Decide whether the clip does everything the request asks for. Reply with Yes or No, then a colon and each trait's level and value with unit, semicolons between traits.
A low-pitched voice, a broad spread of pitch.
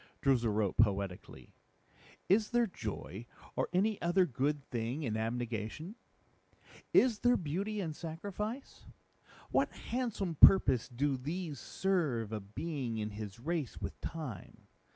No: medium, 145 Hz; wide, 8.6 semitones